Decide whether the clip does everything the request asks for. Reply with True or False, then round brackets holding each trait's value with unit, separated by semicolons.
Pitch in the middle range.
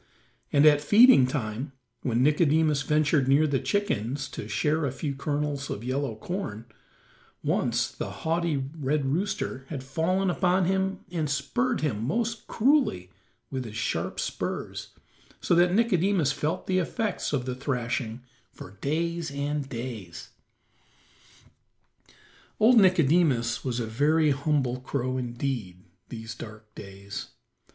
True (145 Hz)